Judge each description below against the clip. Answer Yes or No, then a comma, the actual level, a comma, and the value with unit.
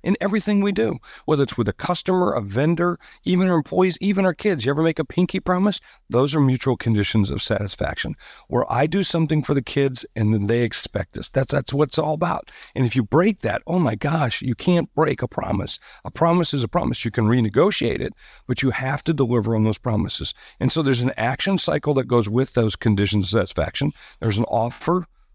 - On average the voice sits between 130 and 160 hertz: Yes, medium, 140 Hz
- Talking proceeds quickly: Yes, fast, 220 wpm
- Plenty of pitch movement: Yes, wide, 6.9 semitones